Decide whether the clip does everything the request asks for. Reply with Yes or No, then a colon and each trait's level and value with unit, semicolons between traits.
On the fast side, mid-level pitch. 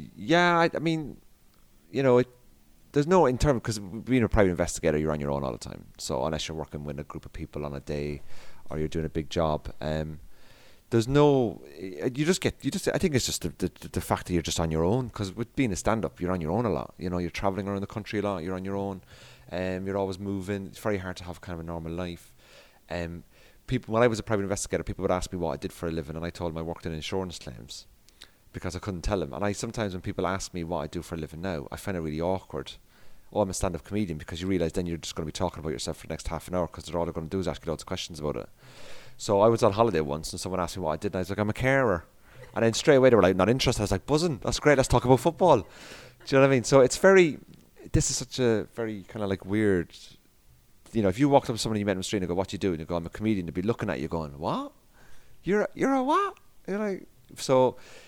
No: fast, 295 wpm; very low, 95 Hz